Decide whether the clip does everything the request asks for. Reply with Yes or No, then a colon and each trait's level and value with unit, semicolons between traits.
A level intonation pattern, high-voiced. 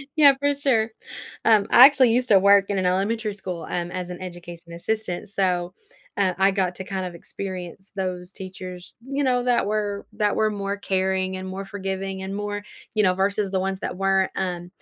Yes: narrow, 2.1 semitones; high, 195 Hz